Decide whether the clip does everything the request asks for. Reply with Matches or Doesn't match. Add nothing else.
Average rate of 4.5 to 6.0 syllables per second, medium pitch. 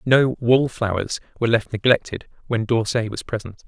Doesn't match